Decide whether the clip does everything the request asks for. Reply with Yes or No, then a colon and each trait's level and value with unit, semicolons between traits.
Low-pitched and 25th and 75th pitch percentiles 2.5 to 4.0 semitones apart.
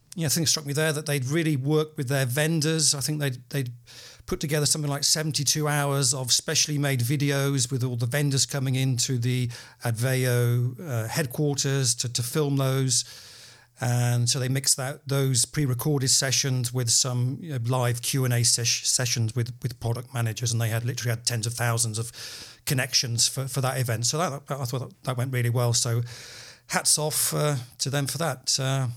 Yes: low, 130 Hz; average, 2.9 semitones